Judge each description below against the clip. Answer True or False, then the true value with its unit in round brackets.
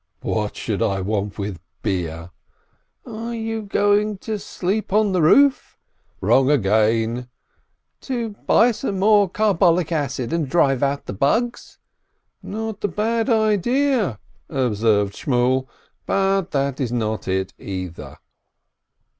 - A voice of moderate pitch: True (165 Hz)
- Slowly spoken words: True (130 wpm)